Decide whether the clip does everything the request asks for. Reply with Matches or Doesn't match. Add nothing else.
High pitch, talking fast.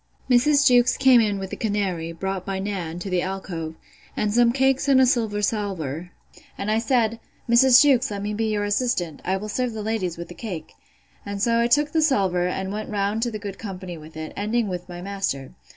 Matches